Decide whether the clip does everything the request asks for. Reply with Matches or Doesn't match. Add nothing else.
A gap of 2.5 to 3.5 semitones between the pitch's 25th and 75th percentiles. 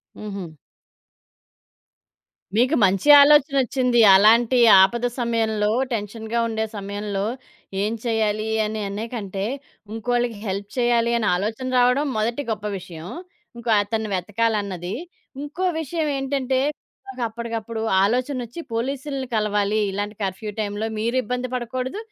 Matches